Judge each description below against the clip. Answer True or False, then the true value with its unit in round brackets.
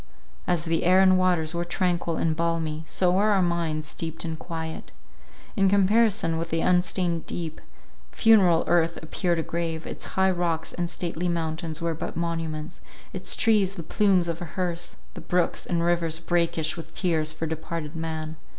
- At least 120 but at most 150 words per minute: False (170 wpm)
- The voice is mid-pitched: True (170 Hz)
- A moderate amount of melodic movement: False (1.7 semitones)